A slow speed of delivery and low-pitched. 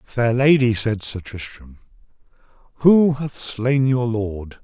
Yes: slow, 130 wpm; low, 120 Hz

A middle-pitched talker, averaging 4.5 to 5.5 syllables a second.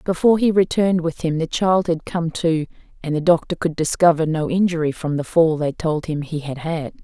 Yes: medium, 165 Hz; 5.4 syllables/s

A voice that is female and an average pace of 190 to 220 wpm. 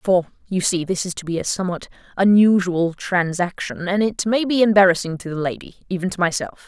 Yes: female; average, 200 wpm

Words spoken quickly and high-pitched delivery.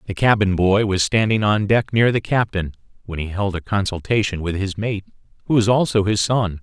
No: fast, 210 wpm; low, 100 Hz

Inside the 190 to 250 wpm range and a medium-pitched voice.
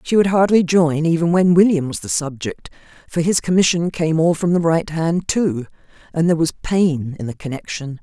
Yes: average, 200 wpm; medium, 165 Hz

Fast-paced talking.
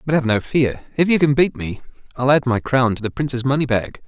Yes: fast, 265 wpm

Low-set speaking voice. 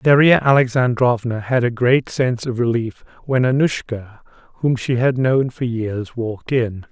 Yes: low, 125 Hz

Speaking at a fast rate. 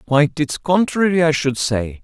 No: average, 175 wpm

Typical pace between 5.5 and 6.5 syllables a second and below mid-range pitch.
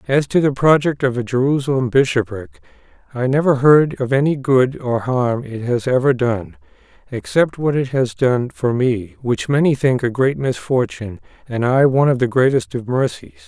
No: 4.9 syllables/s; low, 130 Hz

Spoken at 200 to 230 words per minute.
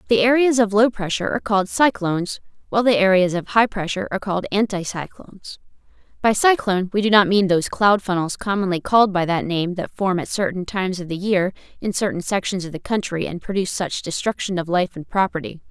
Yes: fast, 205 wpm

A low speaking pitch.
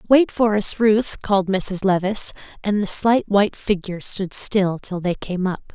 No: high, 200 Hz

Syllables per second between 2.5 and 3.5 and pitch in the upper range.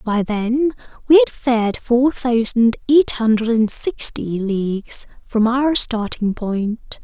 Yes: 3.3 syllables/s; high, 235 Hz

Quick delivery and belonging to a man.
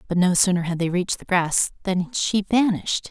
No: fast, 215 wpm; female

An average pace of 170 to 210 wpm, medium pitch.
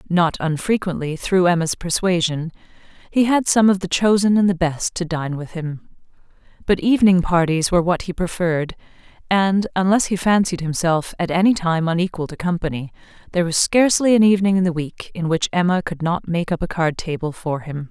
Yes: average, 190 wpm; medium, 175 Hz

